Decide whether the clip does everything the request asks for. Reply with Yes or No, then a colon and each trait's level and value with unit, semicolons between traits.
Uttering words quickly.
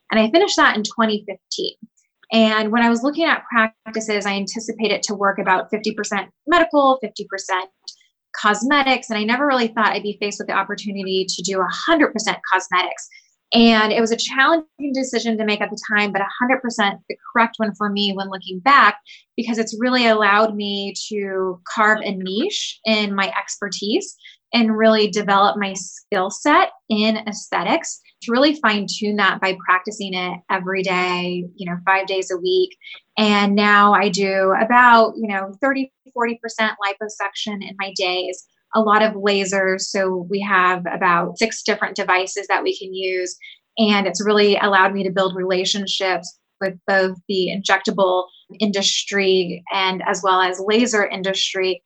No: average, 165 wpm